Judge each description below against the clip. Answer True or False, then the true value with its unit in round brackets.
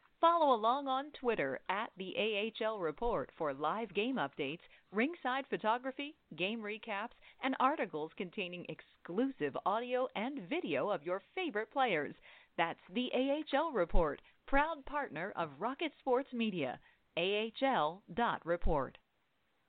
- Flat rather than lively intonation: False (4.7 semitones)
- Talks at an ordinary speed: False (115 wpm)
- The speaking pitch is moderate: False (235 Hz)